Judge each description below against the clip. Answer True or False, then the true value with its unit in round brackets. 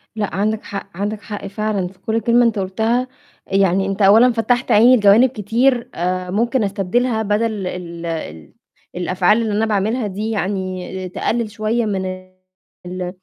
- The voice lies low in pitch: False (205 Hz)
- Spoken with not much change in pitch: False (3.2 semitones)